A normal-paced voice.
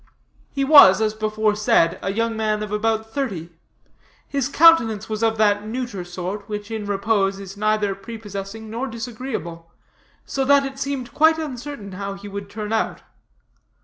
Yes: average, 155 wpm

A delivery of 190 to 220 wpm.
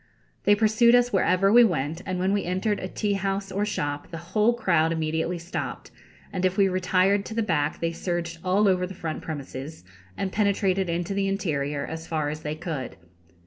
Yes: average, 195 wpm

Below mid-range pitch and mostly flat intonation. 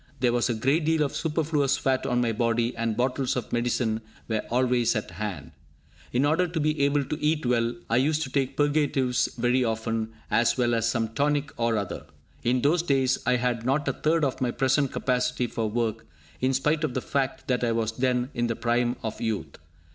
No: low, 125 Hz; average, 3.3 semitones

